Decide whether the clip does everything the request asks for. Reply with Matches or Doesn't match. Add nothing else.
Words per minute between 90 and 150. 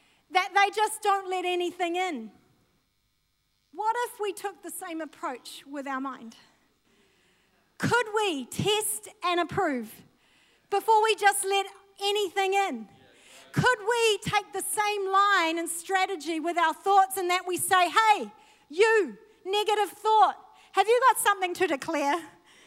Matches